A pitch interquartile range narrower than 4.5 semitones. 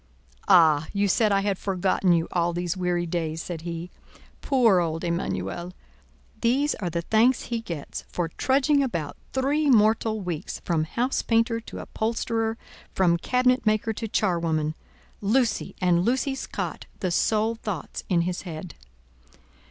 No: average, 5.2 semitones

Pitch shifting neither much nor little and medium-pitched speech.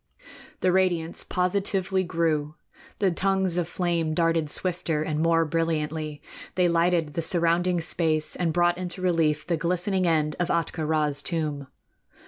No: narrow, 2.3 semitones; medium, 170 Hz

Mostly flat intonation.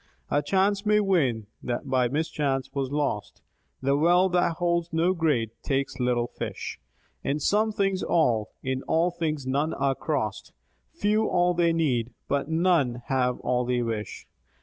No: wide, 5.6 semitones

